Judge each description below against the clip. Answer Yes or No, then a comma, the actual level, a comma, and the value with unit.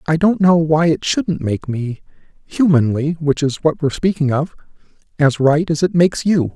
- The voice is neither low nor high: Yes, medium, 155 Hz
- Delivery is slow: No, average, 175 wpm